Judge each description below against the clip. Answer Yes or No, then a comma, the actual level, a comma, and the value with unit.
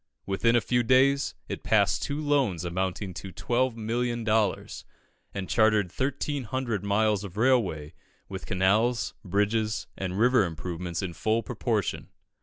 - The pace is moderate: No, slow, 130 wpm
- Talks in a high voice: No, low, 110 Hz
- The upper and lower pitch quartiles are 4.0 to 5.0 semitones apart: Yes, average, 4.3 semitones